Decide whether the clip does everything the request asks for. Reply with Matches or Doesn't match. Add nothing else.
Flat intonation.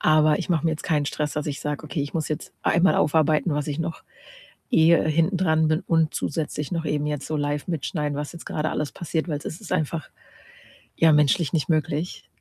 Matches